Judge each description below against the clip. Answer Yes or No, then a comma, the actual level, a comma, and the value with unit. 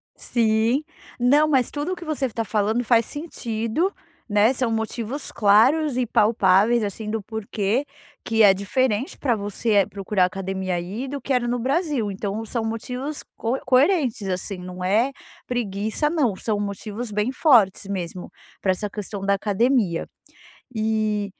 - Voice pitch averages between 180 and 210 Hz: No, high, 220 Hz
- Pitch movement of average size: Yes, average, 4.0 semitones